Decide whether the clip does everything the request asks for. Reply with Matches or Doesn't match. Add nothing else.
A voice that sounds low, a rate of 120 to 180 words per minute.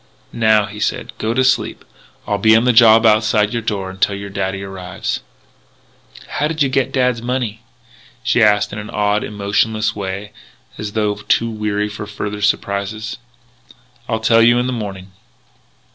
Matches